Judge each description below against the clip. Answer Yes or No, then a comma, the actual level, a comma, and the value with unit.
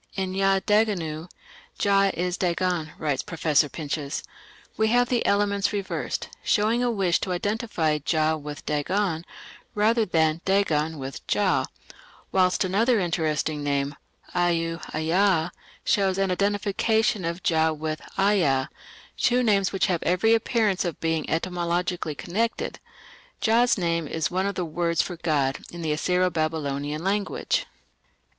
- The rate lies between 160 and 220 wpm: No, slow, 135 wpm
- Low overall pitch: No, medium, 175 Hz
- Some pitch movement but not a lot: Yes, average, 4.1 semitones